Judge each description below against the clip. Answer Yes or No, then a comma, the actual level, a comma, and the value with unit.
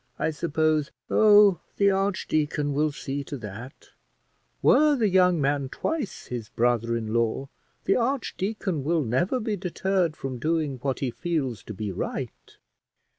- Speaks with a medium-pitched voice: Yes, medium, 155 Hz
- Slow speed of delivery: No, average, 150 wpm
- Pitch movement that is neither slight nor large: No, wide, 6.9 semitones